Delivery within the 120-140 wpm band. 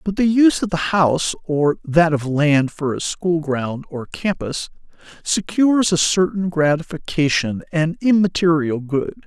No: average, 150 wpm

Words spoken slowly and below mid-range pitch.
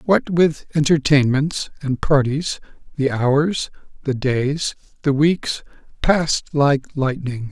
No: slow, 110 wpm; medium, 145 Hz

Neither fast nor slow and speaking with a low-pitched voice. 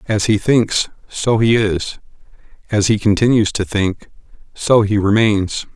Yes: average, 145 wpm; low, 105 Hz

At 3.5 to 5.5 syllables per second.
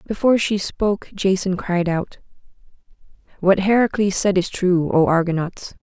Yes: 4.7 syllables/s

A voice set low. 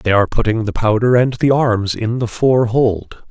Yes: low, 115 Hz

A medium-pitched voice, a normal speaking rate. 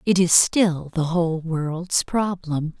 Yes: medium, 170 Hz; average, 150 wpm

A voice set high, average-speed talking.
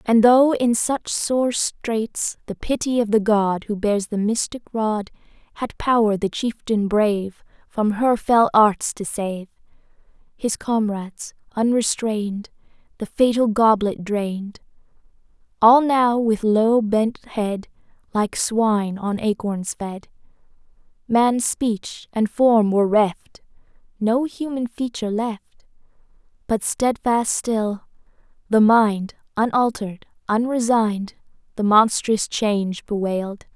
No: high, 220 Hz; slow, 120 wpm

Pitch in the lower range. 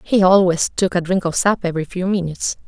No: medium, 180 Hz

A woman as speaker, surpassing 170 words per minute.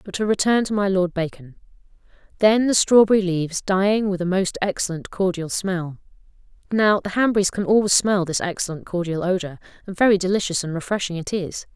Yes: female; average, 180 wpm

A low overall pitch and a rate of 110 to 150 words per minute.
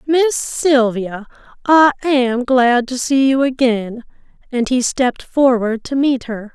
No: very high, 255 Hz; average, 145 wpm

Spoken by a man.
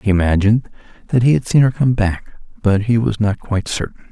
Yes: male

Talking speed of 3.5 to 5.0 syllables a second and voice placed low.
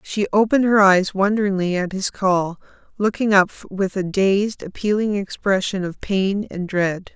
No: 4.5 syllables/s; high, 195 Hz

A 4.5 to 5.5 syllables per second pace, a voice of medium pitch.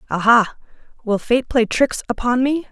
No: 4.7 syllables/s; high, 240 Hz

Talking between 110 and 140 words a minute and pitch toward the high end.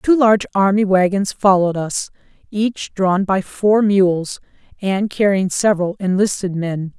Yes: slow, 135 wpm; high, 195 Hz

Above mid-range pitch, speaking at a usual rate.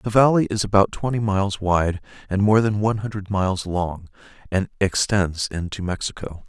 No: low, 100 Hz; average, 165 wpm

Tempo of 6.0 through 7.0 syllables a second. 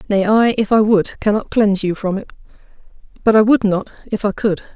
No: 5.6 syllables/s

